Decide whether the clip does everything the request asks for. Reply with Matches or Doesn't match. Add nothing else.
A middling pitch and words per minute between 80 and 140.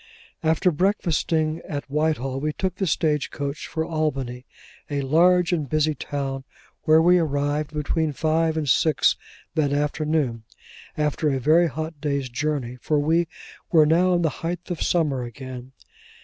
Doesn't match